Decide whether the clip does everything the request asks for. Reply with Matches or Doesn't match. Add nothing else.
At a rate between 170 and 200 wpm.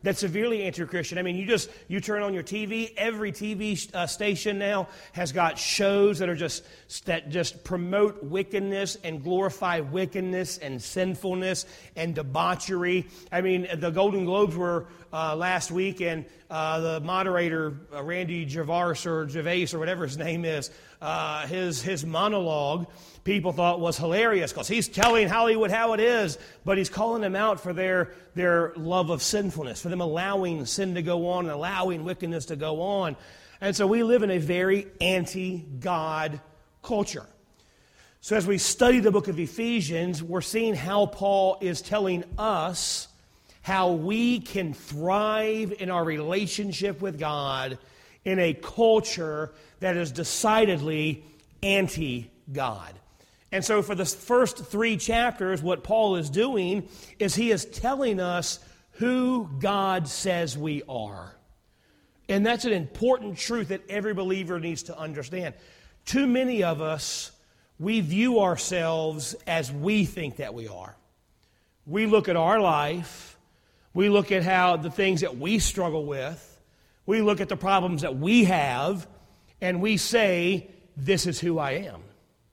Doesn't match